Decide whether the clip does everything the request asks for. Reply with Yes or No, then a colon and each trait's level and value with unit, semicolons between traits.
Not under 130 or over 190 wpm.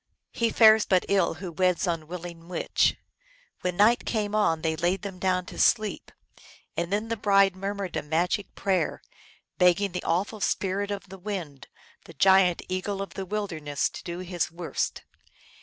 Yes: average, 165 wpm